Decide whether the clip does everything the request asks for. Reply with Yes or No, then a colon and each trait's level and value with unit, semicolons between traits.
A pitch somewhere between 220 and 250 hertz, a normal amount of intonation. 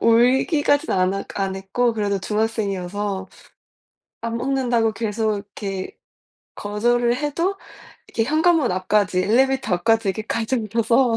Yes: high, 225 Hz; average, 3.6 semitones